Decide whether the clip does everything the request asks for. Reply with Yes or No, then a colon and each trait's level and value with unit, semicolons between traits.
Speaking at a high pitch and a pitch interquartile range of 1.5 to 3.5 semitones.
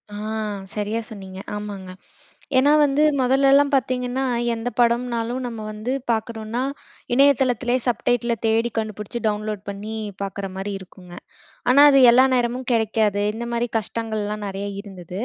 Yes: high, 225 Hz; average, 3.1 semitones